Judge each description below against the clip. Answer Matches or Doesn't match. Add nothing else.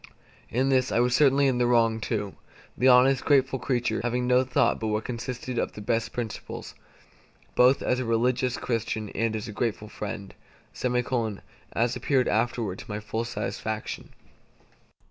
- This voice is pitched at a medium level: Doesn't match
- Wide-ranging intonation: Doesn't match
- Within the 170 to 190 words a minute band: Doesn't match